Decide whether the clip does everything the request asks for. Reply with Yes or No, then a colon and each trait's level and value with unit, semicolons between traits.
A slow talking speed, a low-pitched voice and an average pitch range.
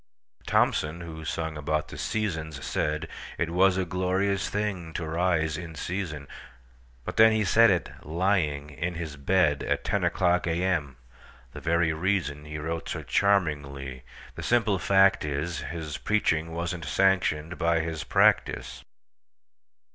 Yes: slow, 120 wpm; very low, 80 Hz; average, 3.6 semitones